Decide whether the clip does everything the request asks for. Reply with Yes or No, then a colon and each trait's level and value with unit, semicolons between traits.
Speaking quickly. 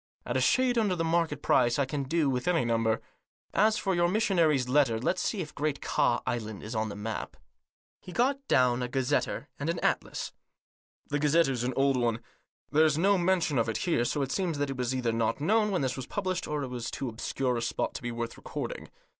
Yes: fast, 225 wpm